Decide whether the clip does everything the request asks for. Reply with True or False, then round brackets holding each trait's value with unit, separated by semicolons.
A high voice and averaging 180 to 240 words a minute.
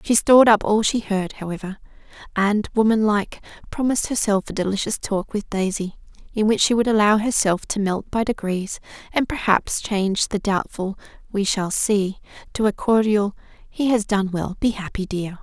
False (205 Hz; 170 wpm)